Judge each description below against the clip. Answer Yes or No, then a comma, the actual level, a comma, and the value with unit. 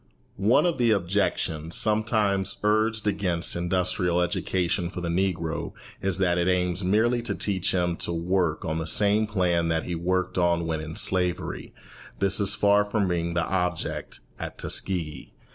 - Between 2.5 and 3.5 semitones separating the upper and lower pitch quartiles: Yes, average, 2.8 semitones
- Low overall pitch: Yes, very low, 90 Hz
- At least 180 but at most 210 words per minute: No, average, 160 wpm